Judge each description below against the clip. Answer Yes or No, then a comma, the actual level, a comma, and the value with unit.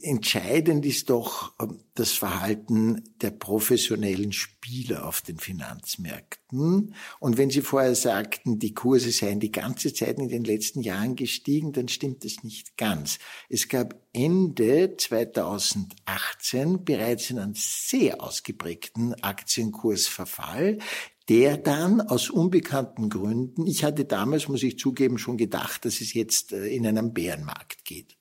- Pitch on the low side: Yes, low, 120 Hz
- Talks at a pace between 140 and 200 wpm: No, average, 130 wpm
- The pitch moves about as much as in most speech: Yes, average, 4.3 semitones